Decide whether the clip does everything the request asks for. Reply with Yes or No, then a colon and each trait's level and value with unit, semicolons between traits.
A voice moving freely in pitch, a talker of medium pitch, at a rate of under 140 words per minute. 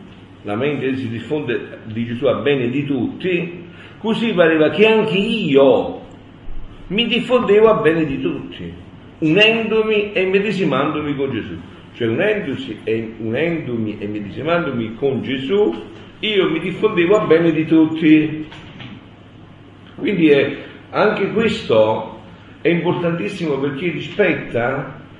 Yes: wide, 8.4 semitones; medium, 150 Hz; slow, 115 wpm